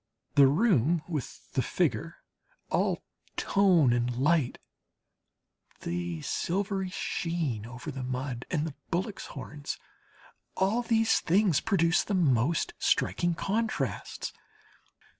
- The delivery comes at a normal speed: No, slow, 105 wpm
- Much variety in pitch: Yes, wide, 6.9 semitones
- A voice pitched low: No, medium, 160 Hz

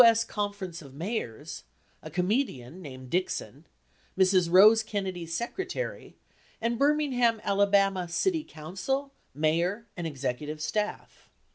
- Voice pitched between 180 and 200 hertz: Yes, high, 190 Hz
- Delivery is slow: Yes, slow, 110 wpm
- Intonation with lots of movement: Yes, wide, 6.1 semitones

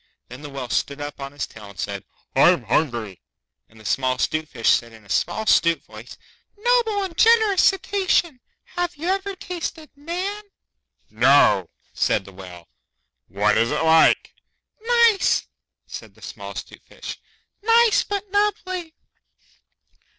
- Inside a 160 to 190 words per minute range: No, average, 145 wpm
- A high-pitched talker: Yes, high, 210 Hz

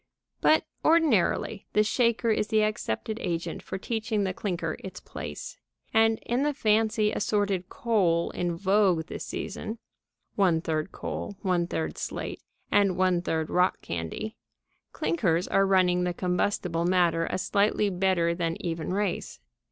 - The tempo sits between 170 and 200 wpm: No, average, 145 wpm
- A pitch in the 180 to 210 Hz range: Yes, medium, 185 Hz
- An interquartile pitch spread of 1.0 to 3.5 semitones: No, average, 3.9 semitones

